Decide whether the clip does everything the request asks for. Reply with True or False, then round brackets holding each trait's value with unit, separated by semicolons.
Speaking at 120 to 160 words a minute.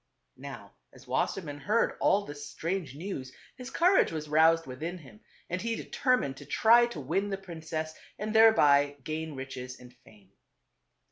True (155 wpm)